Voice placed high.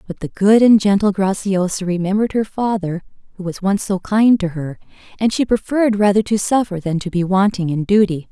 Yes: high, 195 Hz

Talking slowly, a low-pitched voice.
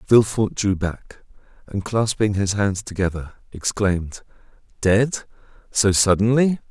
Yes: slow, 90 wpm; low, 105 Hz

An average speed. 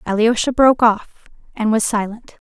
Yes: average, 145 wpm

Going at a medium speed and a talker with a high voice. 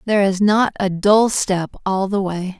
No: fast, 210 wpm; high, 195 Hz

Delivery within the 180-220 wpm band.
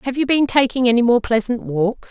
No: fast, 230 wpm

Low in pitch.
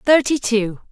No: high, 245 Hz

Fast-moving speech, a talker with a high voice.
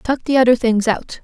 Yes: fast, 240 wpm; high, 240 Hz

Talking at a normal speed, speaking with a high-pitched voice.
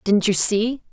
Yes: average, 195 wpm; high, 210 Hz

